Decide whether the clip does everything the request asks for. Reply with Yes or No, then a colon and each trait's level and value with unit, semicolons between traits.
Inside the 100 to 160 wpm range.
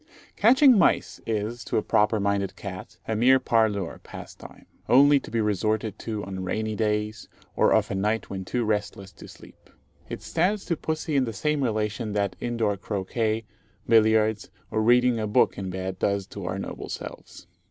No: average, 175 wpm